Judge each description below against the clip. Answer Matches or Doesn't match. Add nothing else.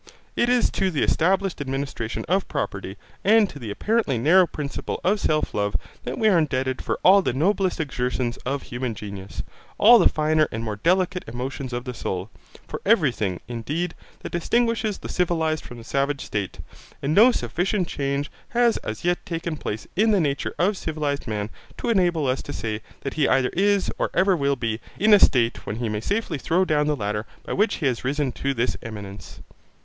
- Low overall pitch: Doesn't match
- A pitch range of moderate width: Doesn't match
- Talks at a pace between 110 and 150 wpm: Doesn't match